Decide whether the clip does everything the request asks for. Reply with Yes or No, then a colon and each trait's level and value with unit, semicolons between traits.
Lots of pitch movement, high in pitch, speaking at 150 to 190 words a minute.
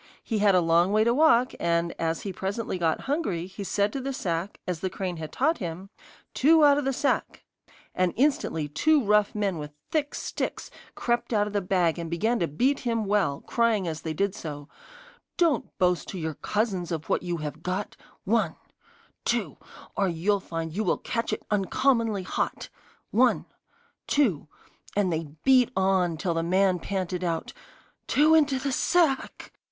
Yes: wide, 5.9 semitones; high, 195 Hz; average, 180 wpm